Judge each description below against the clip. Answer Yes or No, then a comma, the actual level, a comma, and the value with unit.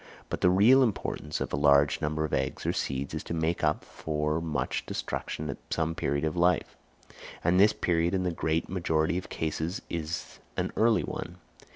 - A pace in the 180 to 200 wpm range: Yes, average, 190 wpm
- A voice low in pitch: Yes, very low, 80 Hz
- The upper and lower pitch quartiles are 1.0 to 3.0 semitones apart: Yes, average, 2.7 semitones